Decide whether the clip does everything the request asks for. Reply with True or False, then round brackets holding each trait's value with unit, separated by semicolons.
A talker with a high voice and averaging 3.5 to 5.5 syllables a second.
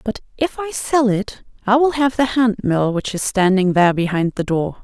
True (215 Hz; 5.0 syllables/s)